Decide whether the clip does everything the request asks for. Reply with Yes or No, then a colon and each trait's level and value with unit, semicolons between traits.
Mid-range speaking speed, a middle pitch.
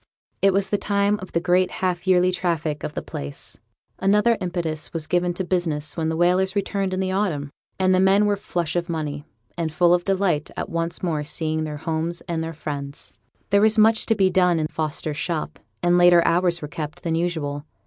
No: fast, 210 wpm; medium, 175 Hz